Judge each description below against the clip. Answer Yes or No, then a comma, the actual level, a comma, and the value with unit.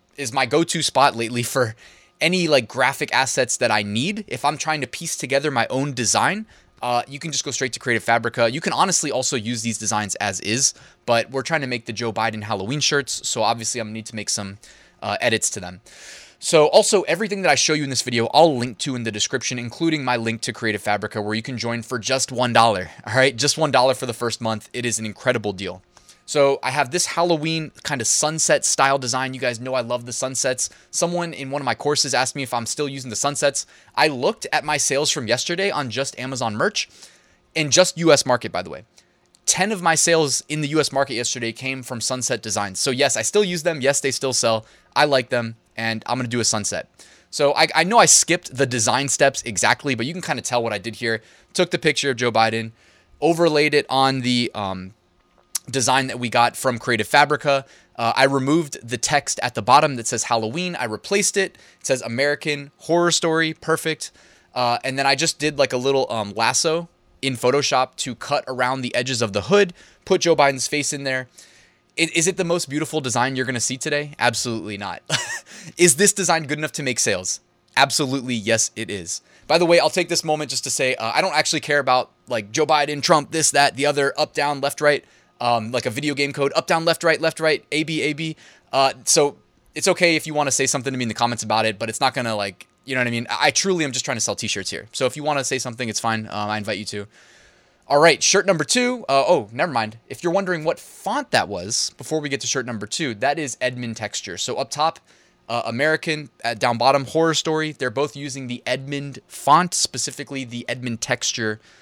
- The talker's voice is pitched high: No, low, 135 Hz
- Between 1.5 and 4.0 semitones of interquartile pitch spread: No, average, 4.6 semitones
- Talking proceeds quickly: Yes, fast, 235 wpm